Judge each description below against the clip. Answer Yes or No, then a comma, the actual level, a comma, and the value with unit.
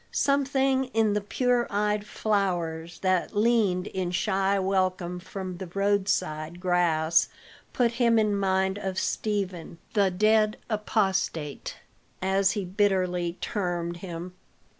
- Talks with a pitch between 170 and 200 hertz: Yes, high, 190 Hz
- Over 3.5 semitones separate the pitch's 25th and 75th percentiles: No, average, 2.9 semitones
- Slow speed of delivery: Yes, slow, 120 wpm